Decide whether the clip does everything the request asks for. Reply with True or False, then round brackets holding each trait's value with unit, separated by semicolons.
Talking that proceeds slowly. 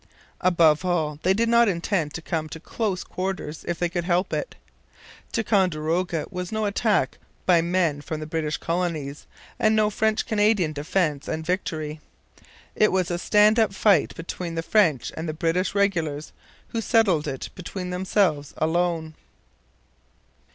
False (150 wpm)